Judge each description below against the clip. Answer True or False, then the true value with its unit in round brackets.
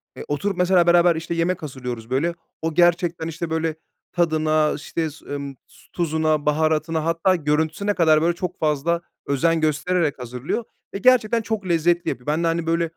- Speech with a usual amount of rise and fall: False (2.1 semitones)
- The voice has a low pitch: False (165 Hz)